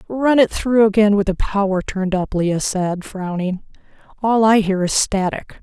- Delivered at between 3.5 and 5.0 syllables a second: Yes, 4.6 syllables/s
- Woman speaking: Yes, female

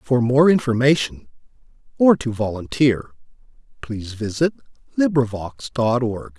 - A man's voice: Yes, male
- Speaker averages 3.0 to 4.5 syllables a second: Yes, 4.4 syllables/s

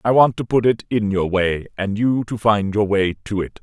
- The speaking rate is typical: No, fast, 265 wpm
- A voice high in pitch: No, low, 105 Hz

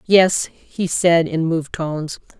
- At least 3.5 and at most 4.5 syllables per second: Yes, 3.9 syllables/s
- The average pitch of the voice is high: No, medium, 165 Hz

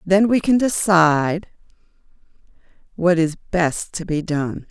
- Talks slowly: Yes, slow, 125 wpm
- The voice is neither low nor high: Yes, medium, 175 Hz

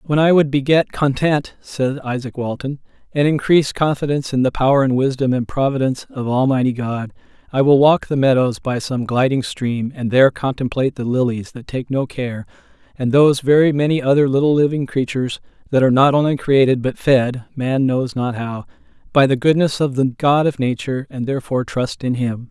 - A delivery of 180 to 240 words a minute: Yes, average, 190 wpm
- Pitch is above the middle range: No, low, 135 Hz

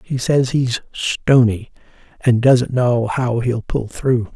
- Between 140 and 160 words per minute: Yes, average, 150 wpm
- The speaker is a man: Yes, male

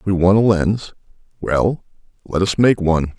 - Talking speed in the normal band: Yes, average, 170 wpm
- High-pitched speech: No, very low, 95 Hz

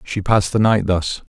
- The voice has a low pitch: Yes, low, 100 Hz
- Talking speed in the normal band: No, fast, 225 wpm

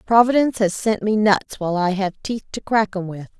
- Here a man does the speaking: No, female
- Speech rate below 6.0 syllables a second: Yes, 5.6 syllables/s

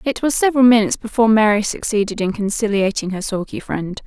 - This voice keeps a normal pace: Yes, average, 175 wpm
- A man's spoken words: No, female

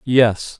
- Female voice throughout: No, male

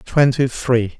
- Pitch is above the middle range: No, low, 125 Hz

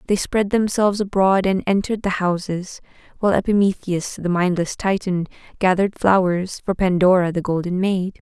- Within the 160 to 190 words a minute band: No, average, 145 wpm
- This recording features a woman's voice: Yes, female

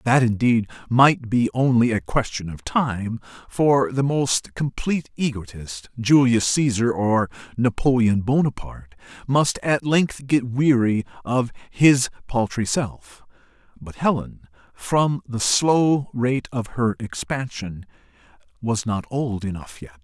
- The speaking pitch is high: No, low, 120 Hz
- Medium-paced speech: No, slow, 125 wpm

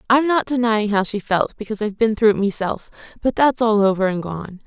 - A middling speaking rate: No, fast, 230 wpm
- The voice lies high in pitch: Yes, high, 215 Hz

